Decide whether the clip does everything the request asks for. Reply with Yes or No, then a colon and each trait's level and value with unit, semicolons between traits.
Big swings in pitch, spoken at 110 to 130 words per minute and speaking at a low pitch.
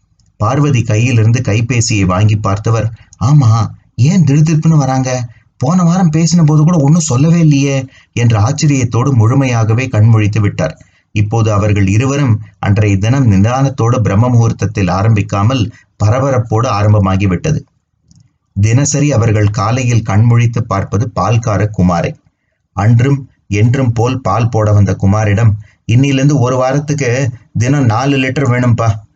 No: average, 4.0 semitones; average, 115 wpm; low, 115 Hz